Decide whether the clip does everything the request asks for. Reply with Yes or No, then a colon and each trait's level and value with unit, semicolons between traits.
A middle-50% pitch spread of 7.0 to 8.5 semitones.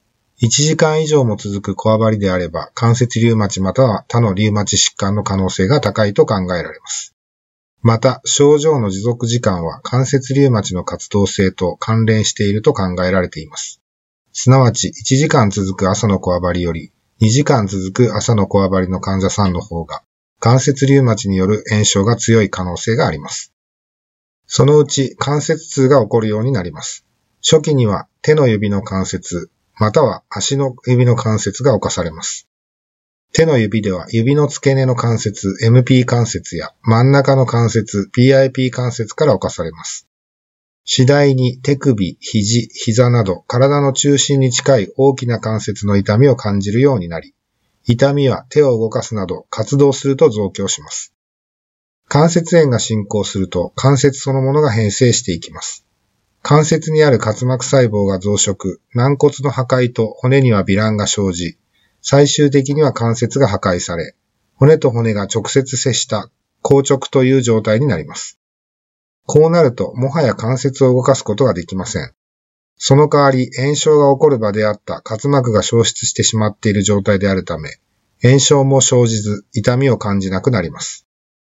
No: average, 5.1 semitones